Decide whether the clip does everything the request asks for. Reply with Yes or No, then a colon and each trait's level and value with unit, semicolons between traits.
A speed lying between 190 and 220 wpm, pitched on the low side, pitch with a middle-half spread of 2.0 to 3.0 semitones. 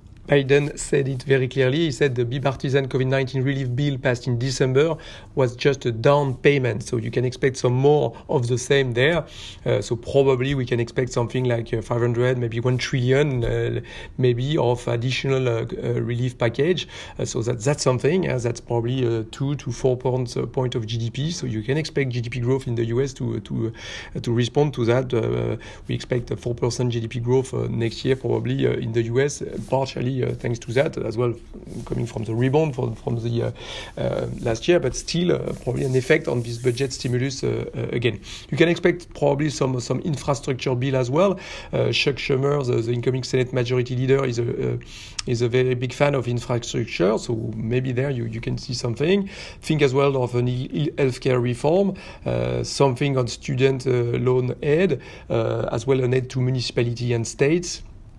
Yes: average, 195 wpm; low, 125 Hz; narrow, 2.4 semitones